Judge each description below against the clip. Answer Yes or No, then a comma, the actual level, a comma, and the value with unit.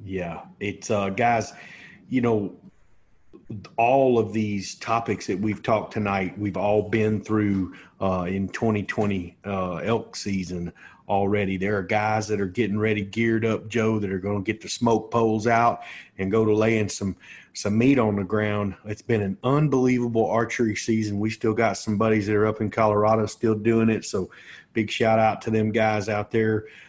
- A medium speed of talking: Yes, average, 180 wpm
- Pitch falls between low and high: No, low, 110 Hz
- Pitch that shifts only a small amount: Yes, narrow, 2.0 semitones